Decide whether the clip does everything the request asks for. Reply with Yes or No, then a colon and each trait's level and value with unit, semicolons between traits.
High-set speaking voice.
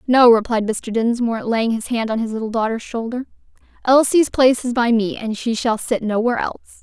Yes: high, 235 Hz